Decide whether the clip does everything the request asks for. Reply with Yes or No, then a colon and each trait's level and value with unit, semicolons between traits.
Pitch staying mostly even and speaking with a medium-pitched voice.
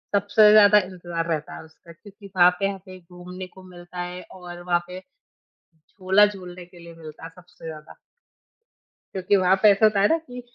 Yes: narrow, 2.3 semitones; medium, 180 Hz